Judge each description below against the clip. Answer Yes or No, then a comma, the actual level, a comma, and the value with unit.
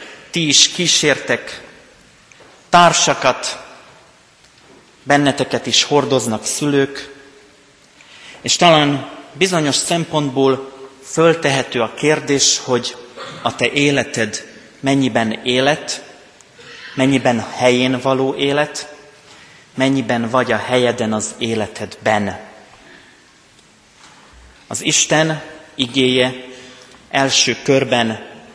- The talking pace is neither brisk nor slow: No, slow, 75 wpm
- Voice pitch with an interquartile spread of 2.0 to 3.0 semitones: Yes, average, 2.7 semitones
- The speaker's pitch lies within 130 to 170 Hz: Yes, low, 135 Hz